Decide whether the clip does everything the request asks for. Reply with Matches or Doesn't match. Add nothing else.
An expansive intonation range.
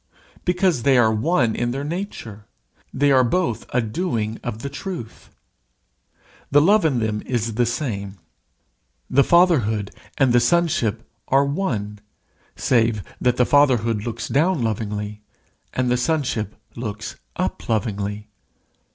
Doesn't match